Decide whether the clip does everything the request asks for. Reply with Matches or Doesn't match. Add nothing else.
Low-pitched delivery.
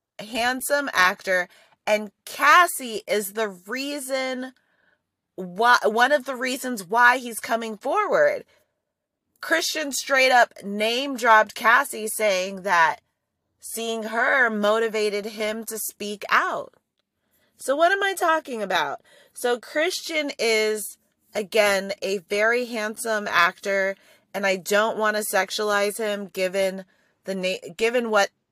Doesn't match